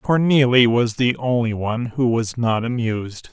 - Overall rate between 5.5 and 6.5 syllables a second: No, 4.6 syllables/s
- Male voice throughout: Yes, male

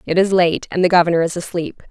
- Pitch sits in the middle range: Yes, medium, 175 Hz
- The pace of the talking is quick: Yes, fast, 250 wpm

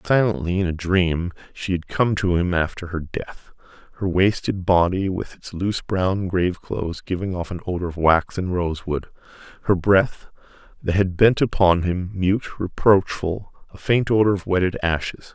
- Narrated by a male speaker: Yes, male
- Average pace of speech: Yes, average, 170 wpm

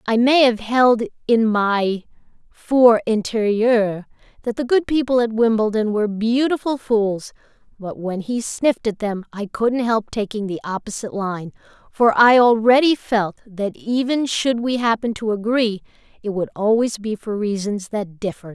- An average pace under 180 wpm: Yes, average, 160 wpm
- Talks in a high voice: Yes, high, 220 Hz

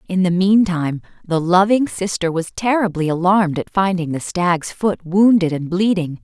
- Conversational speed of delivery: Yes, average, 165 wpm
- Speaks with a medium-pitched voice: Yes, medium, 180 Hz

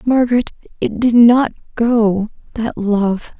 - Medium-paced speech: No, slow, 105 wpm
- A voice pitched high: Yes, high, 225 Hz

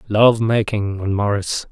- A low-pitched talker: Yes, low, 105 Hz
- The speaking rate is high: No, average, 140 wpm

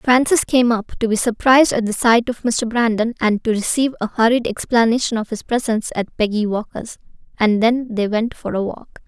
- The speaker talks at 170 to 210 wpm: Yes, fast, 205 wpm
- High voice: Yes, high, 230 Hz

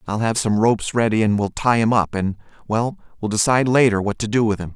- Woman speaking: No, male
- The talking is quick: Yes, fast, 240 wpm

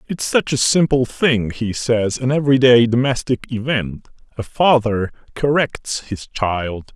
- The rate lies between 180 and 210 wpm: No, average, 140 wpm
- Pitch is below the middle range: Yes, low, 125 Hz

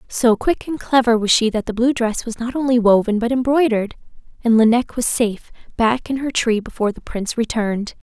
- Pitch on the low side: No, high, 235 Hz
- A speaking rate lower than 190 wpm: No, fast, 205 wpm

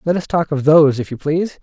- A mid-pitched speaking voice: Yes, medium, 155 Hz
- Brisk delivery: Yes, fast, 295 wpm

